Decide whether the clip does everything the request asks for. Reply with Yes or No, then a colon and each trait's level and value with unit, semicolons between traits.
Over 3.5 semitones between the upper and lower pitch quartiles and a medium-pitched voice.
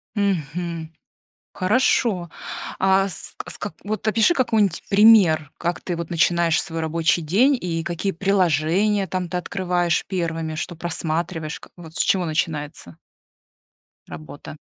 No: average, 3.2 semitones; medium, 175 Hz